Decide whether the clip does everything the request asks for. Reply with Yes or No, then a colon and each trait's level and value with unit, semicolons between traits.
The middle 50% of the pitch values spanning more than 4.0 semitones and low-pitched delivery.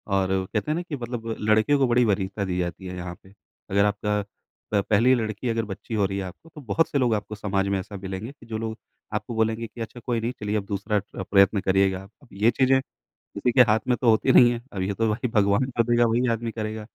No: average, 3.2 semitones; low, 110 Hz